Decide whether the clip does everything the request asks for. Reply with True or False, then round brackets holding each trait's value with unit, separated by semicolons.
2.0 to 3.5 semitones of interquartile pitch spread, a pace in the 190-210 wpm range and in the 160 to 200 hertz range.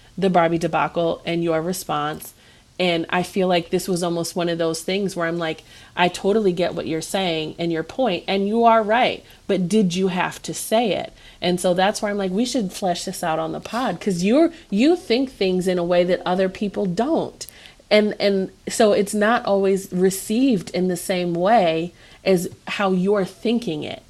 True (3.2 semitones; 205 wpm; 185 Hz)